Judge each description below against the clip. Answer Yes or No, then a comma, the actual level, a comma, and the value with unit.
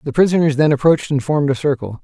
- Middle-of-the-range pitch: Yes, medium, 145 Hz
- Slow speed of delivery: No, fast, 235 wpm